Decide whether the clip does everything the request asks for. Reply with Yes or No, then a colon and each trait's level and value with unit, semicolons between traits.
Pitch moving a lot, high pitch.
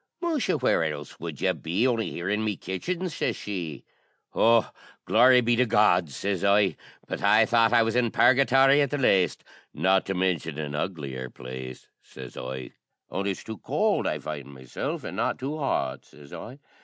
No: wide, 8.4 semitones; low, 100 Hz